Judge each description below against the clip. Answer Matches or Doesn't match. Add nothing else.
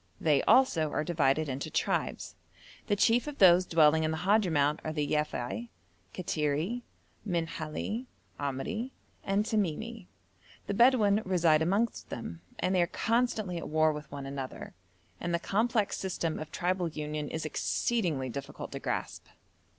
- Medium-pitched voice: Matches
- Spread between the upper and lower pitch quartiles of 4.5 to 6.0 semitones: Matches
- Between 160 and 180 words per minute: Doesn't match